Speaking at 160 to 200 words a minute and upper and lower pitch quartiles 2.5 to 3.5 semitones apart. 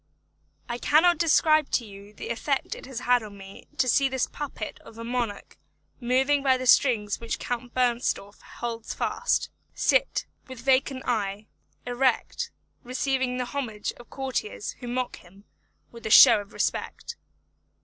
No: average, 150 wpm; average, 3.0 semitones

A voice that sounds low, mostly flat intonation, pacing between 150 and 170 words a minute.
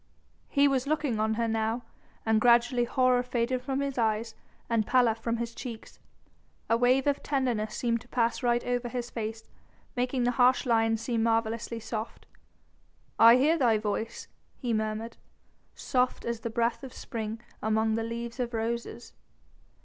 No: high, 235 Hz; narrow, 1.8 semitones; average, 160 wpm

